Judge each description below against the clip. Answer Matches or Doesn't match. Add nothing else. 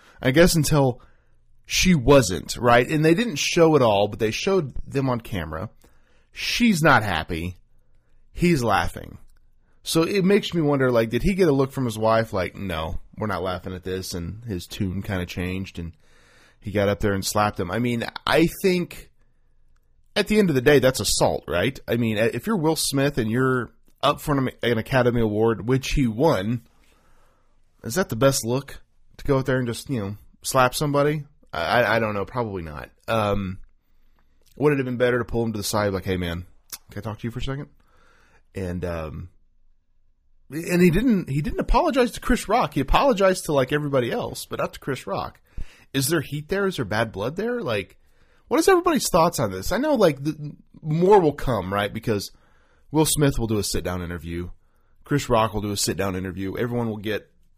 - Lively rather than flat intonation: Matches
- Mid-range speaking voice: Doesn't match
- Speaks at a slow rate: Doesn't match